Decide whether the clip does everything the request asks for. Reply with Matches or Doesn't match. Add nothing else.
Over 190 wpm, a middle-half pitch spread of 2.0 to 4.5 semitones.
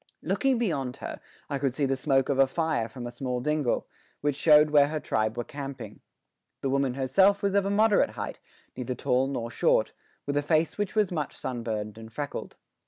Matches